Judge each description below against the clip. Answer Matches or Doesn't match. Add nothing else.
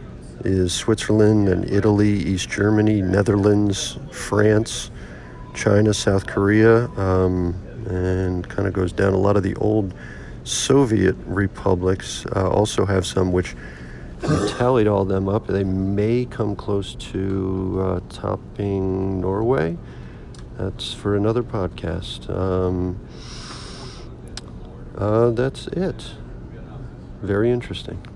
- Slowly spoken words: Matches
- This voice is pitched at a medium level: Doesn't match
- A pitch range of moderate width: Doesn't match